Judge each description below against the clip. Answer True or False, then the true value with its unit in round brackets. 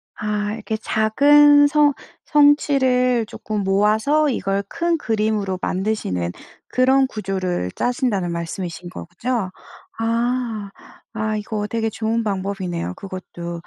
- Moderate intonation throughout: True (4.6 semitones)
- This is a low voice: False (215 Hz)